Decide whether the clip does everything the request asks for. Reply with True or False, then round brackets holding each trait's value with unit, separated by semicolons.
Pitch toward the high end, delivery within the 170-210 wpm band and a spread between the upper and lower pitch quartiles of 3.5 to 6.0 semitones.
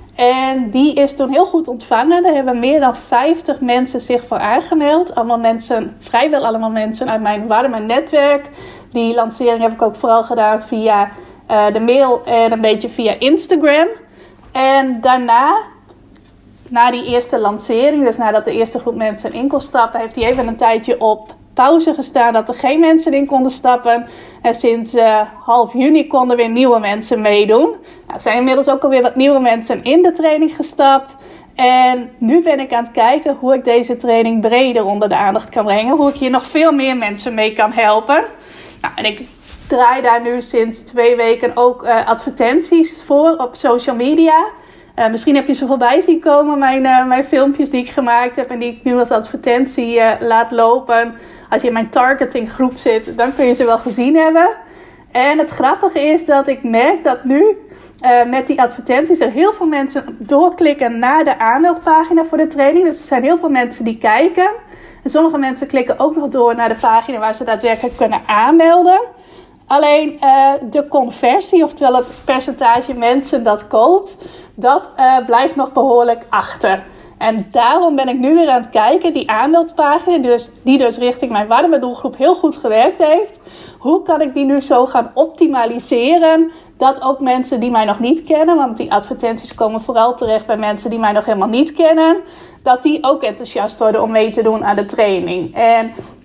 True (255 Hz; 190 wpm; 4.0 semitones)